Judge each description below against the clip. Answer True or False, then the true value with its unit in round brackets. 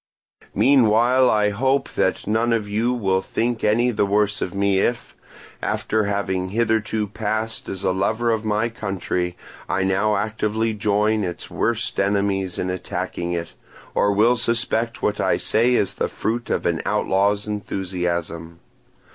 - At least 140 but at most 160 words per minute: True (150 wpm)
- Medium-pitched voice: False (105 Hz)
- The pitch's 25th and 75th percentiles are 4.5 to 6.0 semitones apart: False (2.7 semitones)